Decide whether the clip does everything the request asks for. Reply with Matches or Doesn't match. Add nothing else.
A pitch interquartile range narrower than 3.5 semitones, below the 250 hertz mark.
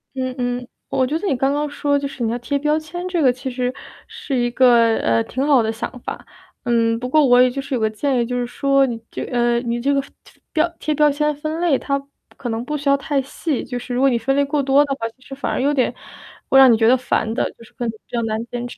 Doesn't match